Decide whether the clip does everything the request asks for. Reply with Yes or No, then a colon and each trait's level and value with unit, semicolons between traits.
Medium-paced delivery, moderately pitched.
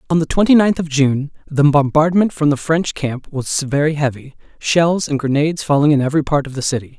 No: fast, 215 wpm; medium, 150 Hz